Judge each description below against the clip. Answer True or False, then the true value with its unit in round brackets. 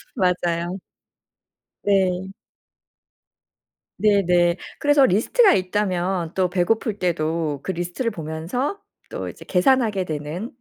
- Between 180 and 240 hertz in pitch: True (185 Hz)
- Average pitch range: True (3.3 semitones)